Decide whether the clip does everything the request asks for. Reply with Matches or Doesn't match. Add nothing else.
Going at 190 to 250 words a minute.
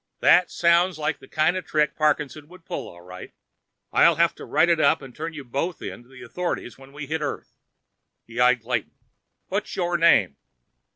Matches